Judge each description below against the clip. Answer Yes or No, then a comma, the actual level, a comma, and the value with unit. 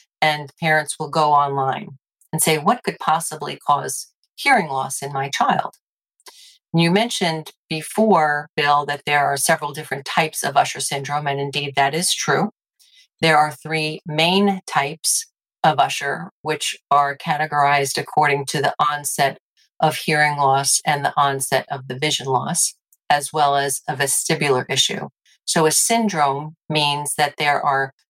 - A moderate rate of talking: Yes, average, 150 wpm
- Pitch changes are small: Yes, narrow, 2.2 semitones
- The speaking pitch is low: No, medium, 150 Hz